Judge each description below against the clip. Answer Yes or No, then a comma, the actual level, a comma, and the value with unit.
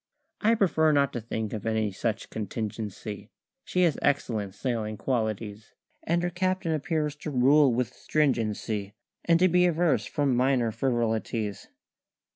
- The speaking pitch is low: Yes, low, 125 Hz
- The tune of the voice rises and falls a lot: Yes, wide, 6.1 semitones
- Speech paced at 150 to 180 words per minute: No, average, 140 wpm